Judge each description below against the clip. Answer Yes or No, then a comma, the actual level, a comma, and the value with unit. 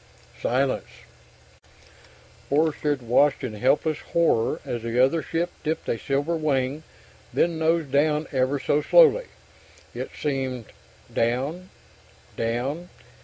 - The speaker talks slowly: Yes, slow, 115 wpm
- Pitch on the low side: No, medium, 145 Hz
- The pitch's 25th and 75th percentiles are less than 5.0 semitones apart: Yes, average, 3.8 semitones